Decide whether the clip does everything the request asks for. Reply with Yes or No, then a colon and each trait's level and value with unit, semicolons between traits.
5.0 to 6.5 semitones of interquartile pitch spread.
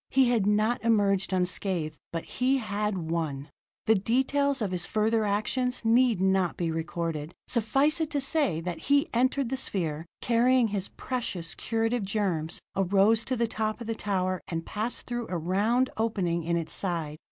Yes: wide, 5.4 semitones